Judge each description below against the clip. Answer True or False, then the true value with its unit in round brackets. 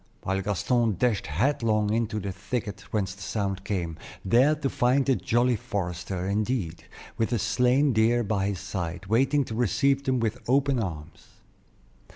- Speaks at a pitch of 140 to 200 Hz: False (110 Hz)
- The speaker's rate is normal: True (160 wpm)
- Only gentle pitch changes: False (4.3 semitones)